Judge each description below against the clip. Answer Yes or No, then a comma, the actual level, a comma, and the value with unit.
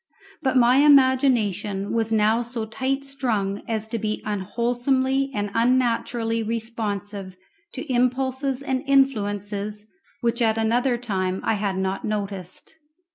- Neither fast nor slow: No, slow, 125 wpm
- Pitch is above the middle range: Yes, high, 230 Hz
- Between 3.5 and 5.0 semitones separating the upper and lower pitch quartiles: Yes, average, 4.0 semitones